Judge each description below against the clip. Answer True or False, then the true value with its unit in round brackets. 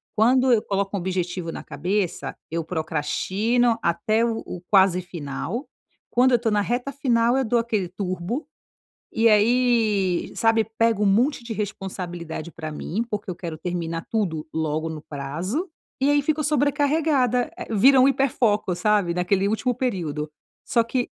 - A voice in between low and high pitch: False (210 Hz)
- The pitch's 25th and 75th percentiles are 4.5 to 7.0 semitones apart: True (5.6 semitones)